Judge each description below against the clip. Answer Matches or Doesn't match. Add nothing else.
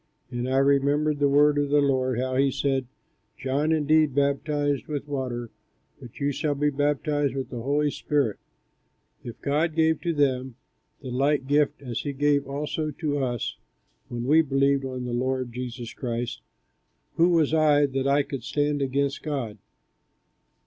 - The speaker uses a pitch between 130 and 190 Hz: Matches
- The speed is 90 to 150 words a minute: Doesn't match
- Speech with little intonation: Matches